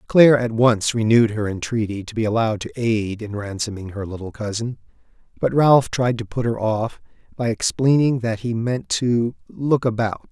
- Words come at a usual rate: Yes, average, 180 wpm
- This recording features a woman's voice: No, male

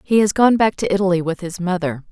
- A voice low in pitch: No, medium, 185 Hz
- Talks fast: Yes, fast, 255 wpm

